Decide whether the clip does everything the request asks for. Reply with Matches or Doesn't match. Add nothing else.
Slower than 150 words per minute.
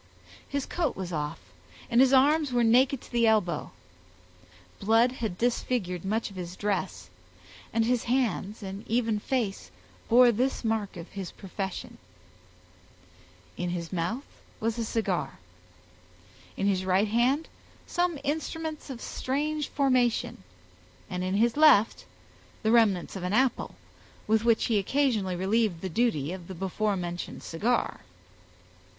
Matches